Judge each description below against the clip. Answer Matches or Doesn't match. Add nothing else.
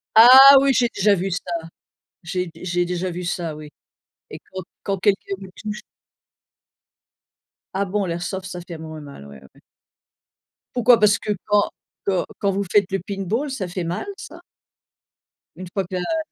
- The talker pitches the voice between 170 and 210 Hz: Matches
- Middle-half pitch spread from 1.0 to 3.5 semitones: Matches